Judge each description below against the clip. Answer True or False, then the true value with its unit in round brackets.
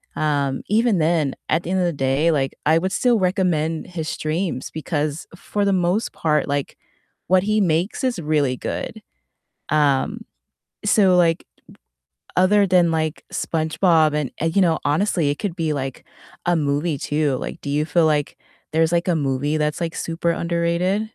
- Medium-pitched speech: True (165 Hz)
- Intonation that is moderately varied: True (3.2 semitones)